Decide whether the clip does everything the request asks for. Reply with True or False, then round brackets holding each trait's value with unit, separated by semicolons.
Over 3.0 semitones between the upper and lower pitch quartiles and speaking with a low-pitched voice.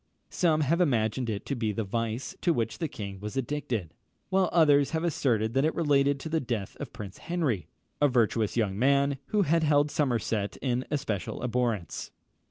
True (5.1 semitones; 130 Hz)